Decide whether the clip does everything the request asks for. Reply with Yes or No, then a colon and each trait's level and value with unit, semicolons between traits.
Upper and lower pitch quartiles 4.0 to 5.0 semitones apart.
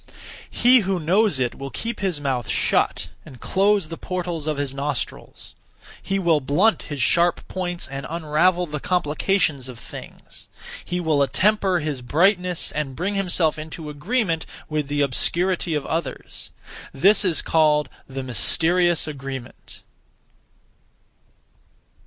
Yes: average, 4.3 semitones